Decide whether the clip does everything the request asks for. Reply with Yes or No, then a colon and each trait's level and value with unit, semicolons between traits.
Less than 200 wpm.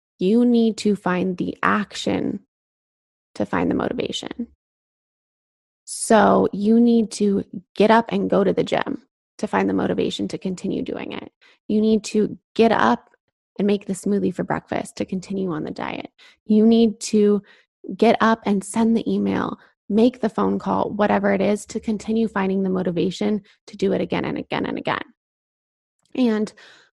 Yes: average, 165 wpm